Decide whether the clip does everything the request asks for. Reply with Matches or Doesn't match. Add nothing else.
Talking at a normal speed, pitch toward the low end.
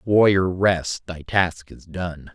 Matches